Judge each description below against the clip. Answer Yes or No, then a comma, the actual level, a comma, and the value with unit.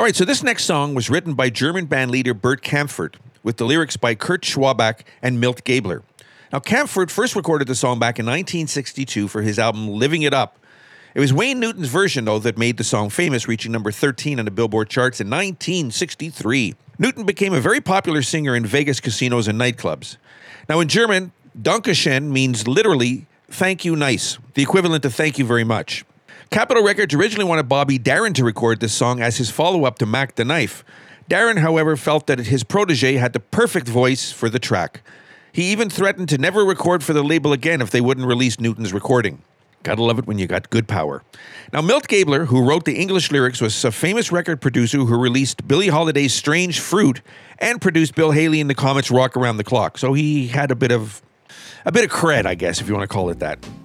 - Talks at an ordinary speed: No, fast, 210 wpm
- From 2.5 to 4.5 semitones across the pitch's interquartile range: No, average, 5.1 semitones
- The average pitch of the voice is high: No, low, 135 Hz